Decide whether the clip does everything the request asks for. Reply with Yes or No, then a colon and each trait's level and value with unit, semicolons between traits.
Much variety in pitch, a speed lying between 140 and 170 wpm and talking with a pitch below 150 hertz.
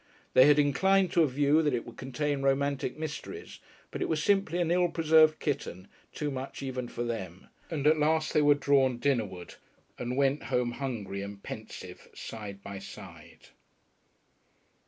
No: average, 4.3 semitones; average, 165 wpm; medium, 140 Hz